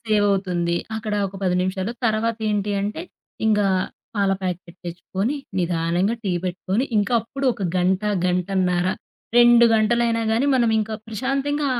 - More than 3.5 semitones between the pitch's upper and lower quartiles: Yes, average, 3.9 semitones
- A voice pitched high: Yes, high, 205 Hz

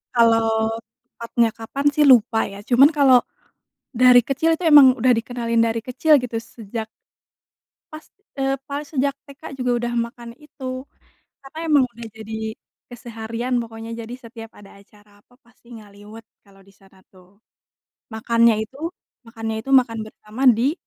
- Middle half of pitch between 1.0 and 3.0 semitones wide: Yes, narrow, 2.6 semitones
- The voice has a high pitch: Yes, high, 235 Hz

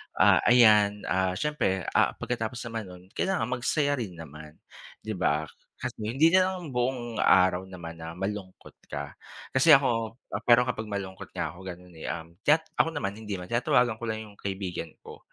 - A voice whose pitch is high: No, low, 105 Hz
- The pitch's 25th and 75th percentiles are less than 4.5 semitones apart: No, average, 5.1 semitones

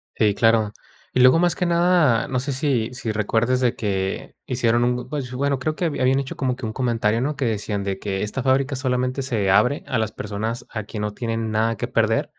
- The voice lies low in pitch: Yes, low, 120 Hz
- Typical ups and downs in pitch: Yes, average, 3.3 semitones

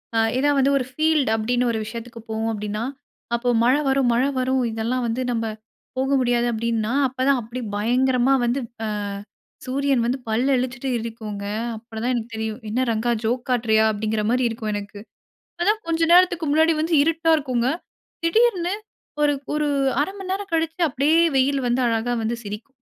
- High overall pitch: Yes, very high, 250 Hz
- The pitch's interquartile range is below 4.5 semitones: Yes, average, 3.9 semitones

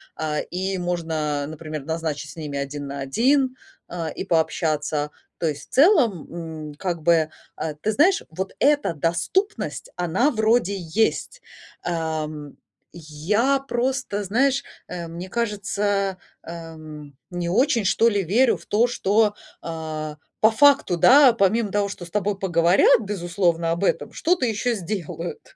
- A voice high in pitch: No, medium, 180 Hz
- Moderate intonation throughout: No, wide, 6.0 semitones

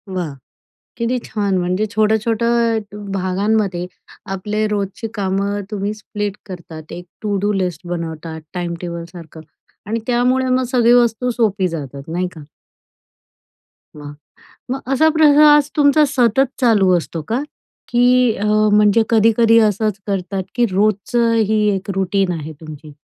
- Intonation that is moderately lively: Yes, average, 4.3 semitones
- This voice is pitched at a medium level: No, high, 205 Hz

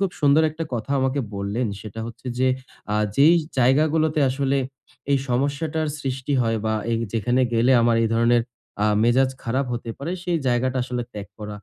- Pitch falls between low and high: No, low, 130 Hz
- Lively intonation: No, average, 3.5 semitones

